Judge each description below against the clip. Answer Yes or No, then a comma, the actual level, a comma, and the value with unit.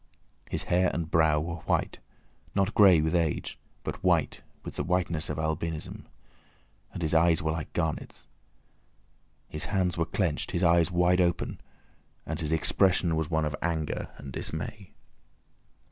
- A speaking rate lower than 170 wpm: Yes, average, 145 wpm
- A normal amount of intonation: No, narrow, 2.0 semitones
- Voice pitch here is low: Yes, very low, 85 Hz